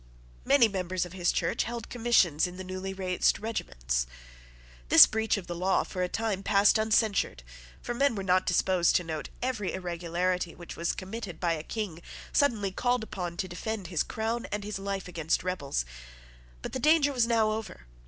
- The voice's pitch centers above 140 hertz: Yes, high, 190 Hz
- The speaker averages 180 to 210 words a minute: Yes, average, 185 wpm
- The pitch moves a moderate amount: Yes, average, 4.0 semitones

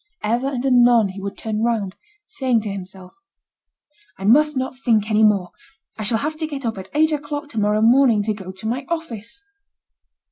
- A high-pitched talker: Yes, high, 230 Hz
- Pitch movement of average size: Yes, average, 4.6 semitones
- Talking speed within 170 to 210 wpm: Yes, average, 190 wpm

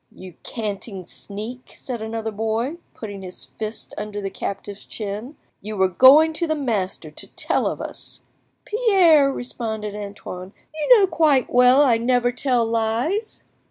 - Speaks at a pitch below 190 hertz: No, high, 230 Hz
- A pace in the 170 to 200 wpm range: No, average, 150 wpm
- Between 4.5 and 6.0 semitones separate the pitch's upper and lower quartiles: Yes, average, 4.9 semitones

